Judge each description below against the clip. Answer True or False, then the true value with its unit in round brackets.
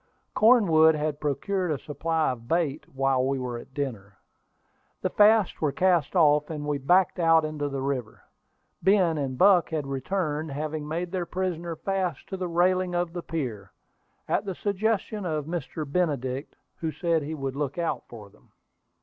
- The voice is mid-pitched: True (160 Hz)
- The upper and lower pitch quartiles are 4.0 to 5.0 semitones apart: True (4.3 semitones)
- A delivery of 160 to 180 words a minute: True (170 wpm)